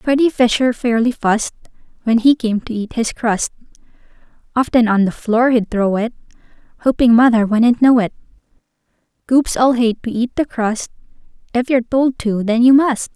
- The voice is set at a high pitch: Yes, high, 235 Hz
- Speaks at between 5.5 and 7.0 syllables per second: No, 5.0 syllables/s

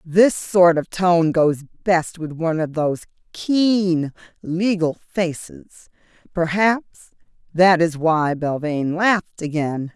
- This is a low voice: No, medium, 170 Hz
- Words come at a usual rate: No, slow, 120 wpm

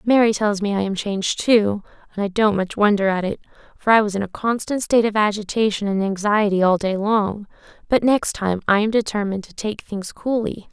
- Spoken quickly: Yes, fast, 215 wpm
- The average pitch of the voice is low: No, high, 205 Hz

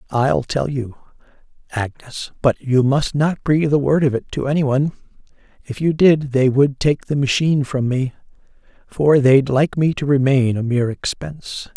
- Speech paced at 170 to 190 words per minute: Yes, average, 180 wpm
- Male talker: Yes, male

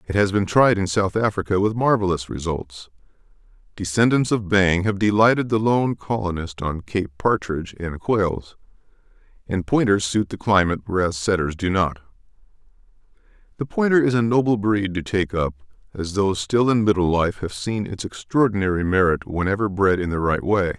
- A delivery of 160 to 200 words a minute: Yes, average, 165 wpm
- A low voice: Yes, low, 100 Hz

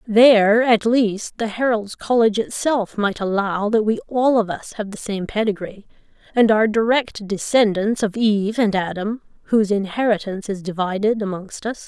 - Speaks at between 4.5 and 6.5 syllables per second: Yes, 5.0 syllables/s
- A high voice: Yes, high, 215 Hz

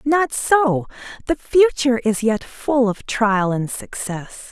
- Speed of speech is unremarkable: Yes, average, 145 wpm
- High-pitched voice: Yes, high, 240 Hz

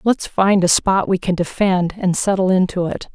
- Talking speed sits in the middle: No, fast, 210 wpm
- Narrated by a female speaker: Yes, female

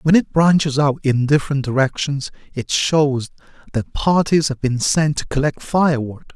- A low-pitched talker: No, medium, 145 Hz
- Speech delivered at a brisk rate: No, average, 160 wpm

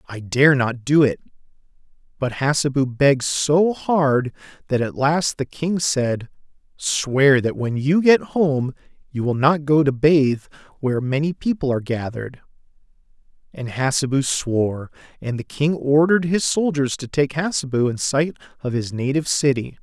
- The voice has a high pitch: No, medium, 140 Hz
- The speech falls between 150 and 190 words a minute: Yes, average, 155 wpm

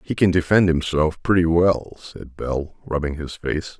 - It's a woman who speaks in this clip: No, male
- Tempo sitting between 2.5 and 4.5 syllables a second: Yes, 4.4 syllables/s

